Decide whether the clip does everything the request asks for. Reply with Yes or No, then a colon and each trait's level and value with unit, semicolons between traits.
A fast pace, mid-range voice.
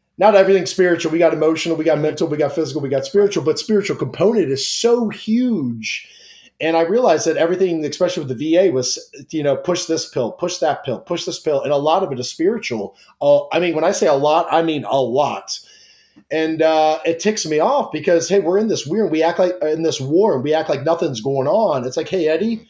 Yes: fast, 240 wpm; medium, 165 Hz